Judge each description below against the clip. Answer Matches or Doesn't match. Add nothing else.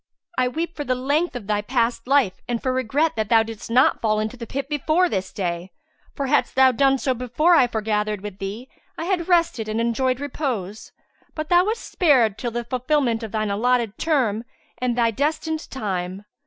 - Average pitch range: Matches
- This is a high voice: Matches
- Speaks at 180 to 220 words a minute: Matches